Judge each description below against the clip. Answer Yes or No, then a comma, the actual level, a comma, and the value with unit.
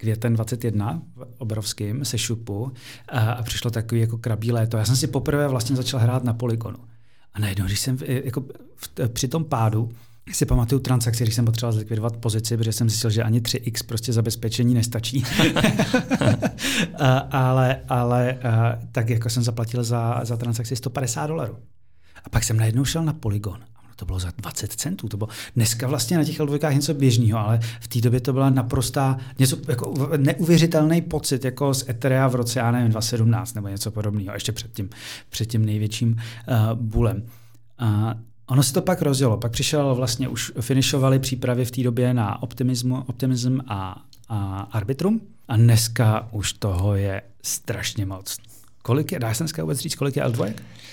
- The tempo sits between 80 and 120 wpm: No, fast, 170 wpm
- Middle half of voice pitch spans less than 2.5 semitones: No, average, 2.8 semitones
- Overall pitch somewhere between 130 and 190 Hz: No, low, 120 Hz